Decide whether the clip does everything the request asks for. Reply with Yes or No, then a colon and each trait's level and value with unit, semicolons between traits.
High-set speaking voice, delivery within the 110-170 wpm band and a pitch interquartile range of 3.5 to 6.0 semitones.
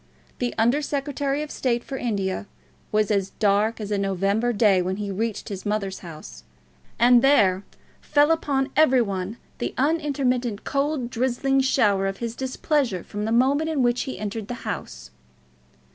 Yes: high, 235 Hz; average, 160 wpm; average, 5.1 semitones